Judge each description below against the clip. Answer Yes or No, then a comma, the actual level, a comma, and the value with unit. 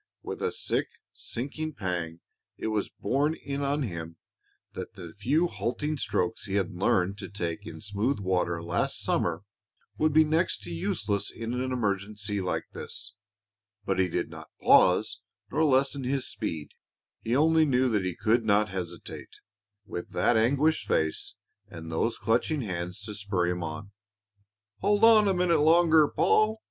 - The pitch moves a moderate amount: No, wide, 7.5 semitones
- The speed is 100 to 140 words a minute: No, average, 160 wpm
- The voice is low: Yes, low, 105 Hz